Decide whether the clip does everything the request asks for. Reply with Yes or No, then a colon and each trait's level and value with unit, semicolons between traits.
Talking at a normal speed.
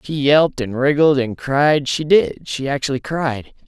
Yes: average, 145 wpm